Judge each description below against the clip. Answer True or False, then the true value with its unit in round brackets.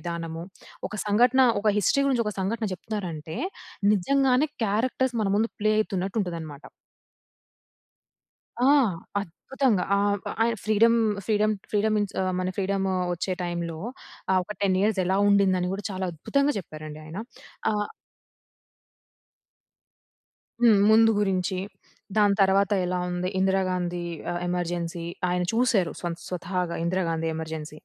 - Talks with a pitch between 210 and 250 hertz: False (190 Hz)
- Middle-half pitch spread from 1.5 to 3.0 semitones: False (3.4 semitones)